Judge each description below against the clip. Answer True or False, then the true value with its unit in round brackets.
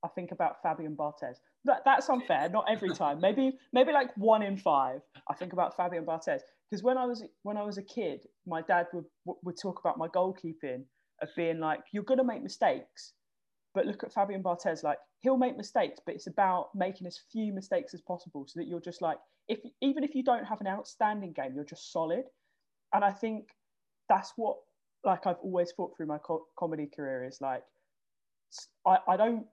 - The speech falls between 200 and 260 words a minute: True (205 wpm)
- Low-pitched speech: False (185 Hz)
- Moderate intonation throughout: True (4.9 semitones)